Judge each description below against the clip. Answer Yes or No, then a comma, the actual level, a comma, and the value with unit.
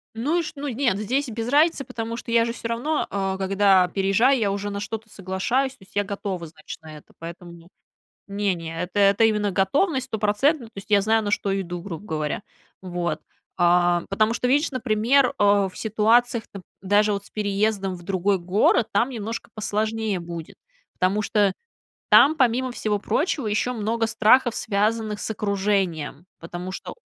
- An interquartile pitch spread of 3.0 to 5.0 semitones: Yes, average, 3.3 semitones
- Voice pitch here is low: No, high, 205 Hz